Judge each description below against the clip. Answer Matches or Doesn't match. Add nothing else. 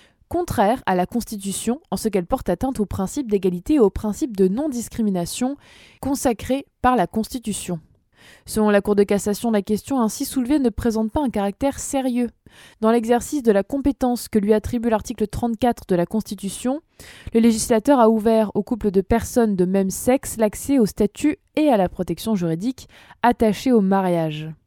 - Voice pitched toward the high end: Matches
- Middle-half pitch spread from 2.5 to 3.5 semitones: Doesn't match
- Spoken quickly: Doesn't match